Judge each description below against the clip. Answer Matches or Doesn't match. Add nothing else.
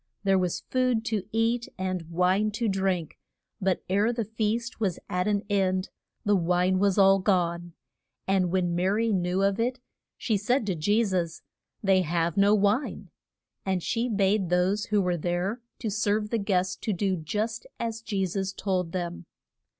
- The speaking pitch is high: Matches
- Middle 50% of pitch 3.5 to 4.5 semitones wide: Doesn't match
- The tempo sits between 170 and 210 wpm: Matches